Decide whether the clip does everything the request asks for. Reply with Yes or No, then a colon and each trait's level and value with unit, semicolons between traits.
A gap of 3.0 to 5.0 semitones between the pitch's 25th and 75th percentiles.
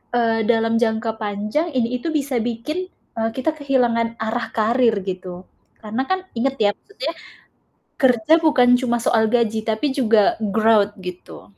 No: narrow, 2.6 semitones